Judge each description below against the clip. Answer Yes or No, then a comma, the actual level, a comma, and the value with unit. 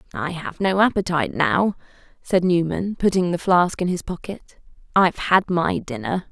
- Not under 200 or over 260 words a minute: No, average, 160 wpm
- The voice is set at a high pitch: No, medium, 175 Hz